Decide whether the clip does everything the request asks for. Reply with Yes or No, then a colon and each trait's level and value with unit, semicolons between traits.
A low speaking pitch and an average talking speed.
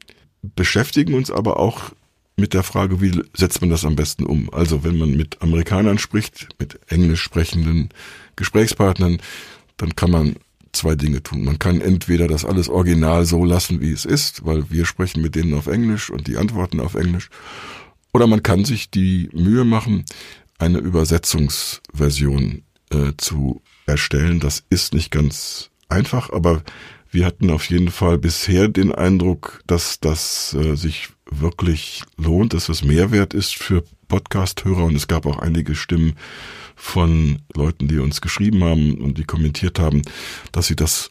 Yes: very low, 85 Hz; average, 160 wpm